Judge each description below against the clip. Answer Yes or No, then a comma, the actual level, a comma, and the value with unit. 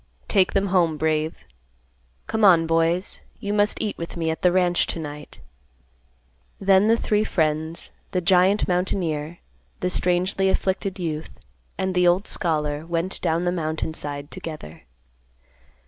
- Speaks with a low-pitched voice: No, medium, 175 Hz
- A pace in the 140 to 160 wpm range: Yes, average, 145 wpm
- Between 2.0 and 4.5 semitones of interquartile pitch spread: Yes, average, 3.1 semitones